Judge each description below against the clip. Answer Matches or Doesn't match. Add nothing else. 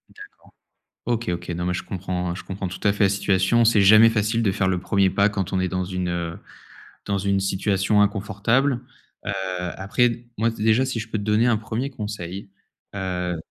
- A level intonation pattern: Doesn't match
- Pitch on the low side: Matches